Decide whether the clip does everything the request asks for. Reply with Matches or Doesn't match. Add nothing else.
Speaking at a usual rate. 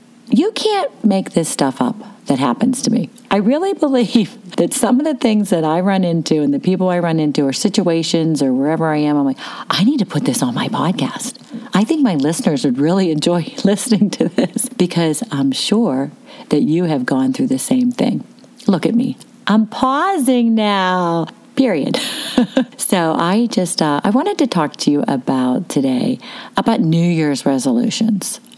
Matches